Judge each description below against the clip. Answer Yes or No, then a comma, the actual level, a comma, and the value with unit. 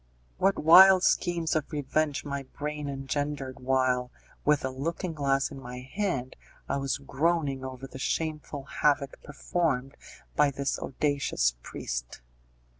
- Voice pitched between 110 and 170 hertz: Yes, medium, 140 Hz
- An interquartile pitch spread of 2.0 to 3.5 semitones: Yes, narrow, 2.6 semitones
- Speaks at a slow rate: Yes, slow, 130 wpm